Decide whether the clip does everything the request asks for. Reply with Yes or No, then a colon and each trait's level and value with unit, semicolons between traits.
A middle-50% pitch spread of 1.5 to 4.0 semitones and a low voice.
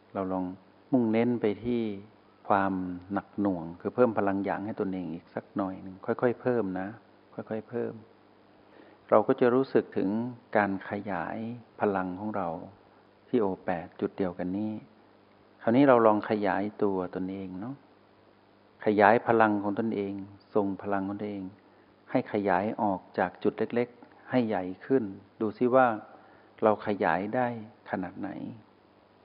Yes: narrow, 2.5 semitones; low, 105 Hz